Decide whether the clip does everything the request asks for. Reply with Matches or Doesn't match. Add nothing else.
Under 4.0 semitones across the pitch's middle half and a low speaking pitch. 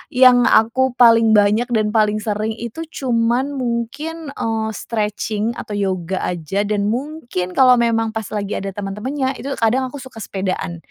Doesn't match